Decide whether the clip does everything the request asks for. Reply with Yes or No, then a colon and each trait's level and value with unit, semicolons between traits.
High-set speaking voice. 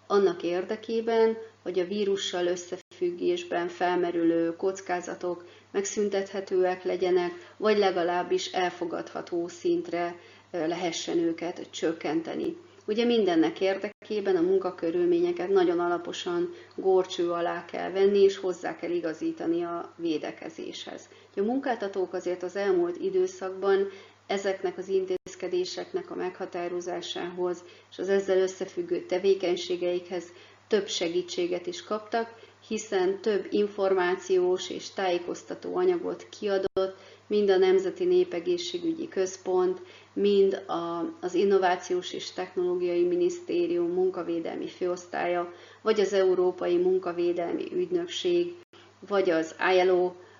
Yes: high, 195 Hz